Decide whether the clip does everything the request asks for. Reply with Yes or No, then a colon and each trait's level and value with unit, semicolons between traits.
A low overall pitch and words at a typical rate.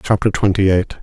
Yes: low, 100 Hz; average, 175 wpm